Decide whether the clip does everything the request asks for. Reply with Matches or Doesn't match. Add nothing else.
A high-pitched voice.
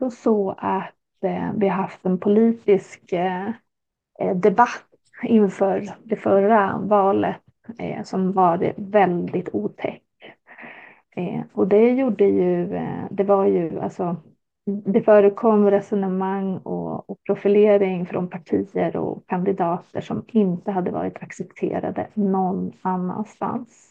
Matches